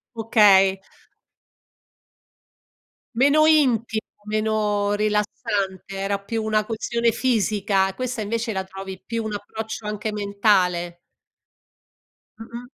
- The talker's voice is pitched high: Yes, high, 210 Hz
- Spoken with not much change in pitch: Yes, narrow, 2.3 semitones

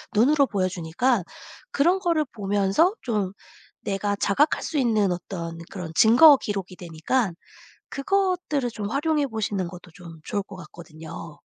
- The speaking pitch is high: Yes, high, 205 Hz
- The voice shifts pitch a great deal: Yes, wide, 7.3 semitones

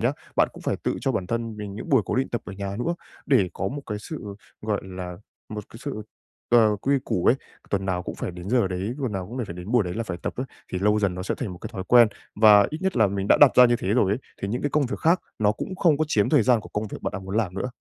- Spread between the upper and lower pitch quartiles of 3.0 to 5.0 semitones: Yes, average, 4.3 semitones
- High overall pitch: No, low, 105 Hz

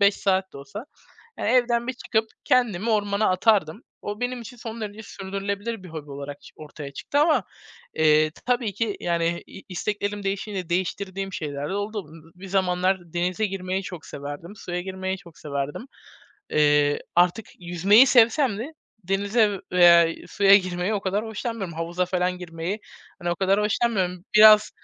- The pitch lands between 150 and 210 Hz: Yes, high, 190 Hz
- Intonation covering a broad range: No, average, 3.6 semitones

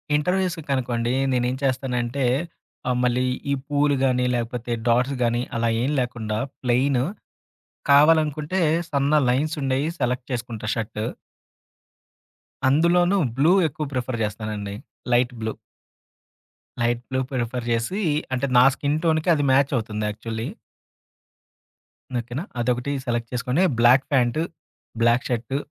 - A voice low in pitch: Yes, low, 125 Hz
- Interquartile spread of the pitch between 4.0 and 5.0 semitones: No, average, 3.2 semitones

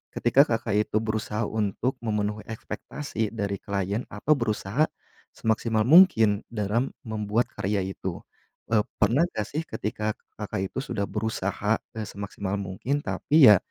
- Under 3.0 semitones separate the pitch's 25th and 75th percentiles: Yes, narrow, 2.4 semitones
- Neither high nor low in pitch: No, low, 110 Hz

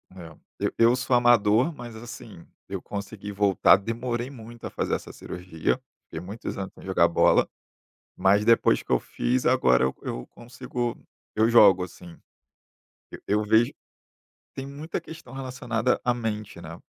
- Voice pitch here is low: Yes, low, 115 Hz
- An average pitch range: Yes, average, 3.8 semitones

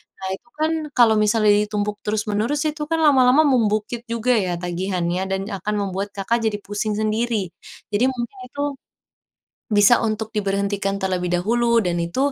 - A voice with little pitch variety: No, average, 3.4 semitones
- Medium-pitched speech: No, high, 215 Hz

